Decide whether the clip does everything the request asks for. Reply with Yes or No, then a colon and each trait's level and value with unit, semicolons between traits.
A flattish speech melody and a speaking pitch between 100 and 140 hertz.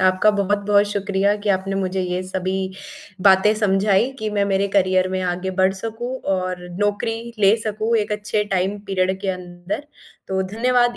No: narrow, 2.0 semitones; high, 195 Hz